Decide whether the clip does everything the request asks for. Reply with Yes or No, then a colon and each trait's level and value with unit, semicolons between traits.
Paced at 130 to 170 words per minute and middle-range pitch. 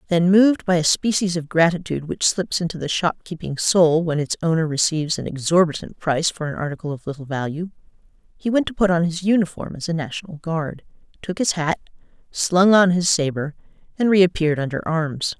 No: average, 185 wpm; medium, 170 Hz